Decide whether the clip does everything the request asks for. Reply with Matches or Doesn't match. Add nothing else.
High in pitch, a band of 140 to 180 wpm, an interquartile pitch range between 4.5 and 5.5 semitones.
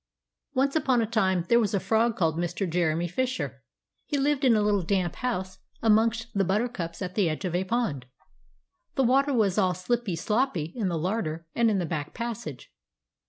Doesn't match